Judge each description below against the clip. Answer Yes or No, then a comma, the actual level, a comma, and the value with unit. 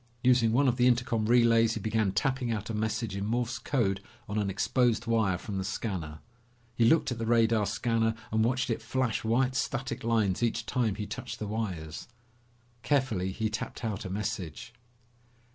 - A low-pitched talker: Yes, low, 115 Hz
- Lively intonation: No, narrow, 2.6 semitones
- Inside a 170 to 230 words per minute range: Yes, average, 180 wpm